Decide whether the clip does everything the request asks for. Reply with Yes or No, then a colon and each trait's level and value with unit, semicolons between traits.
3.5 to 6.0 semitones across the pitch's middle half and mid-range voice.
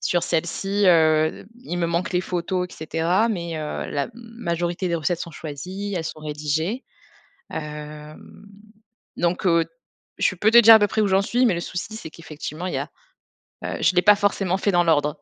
Yes: average, 3.9 semitones; medium, 175 Hz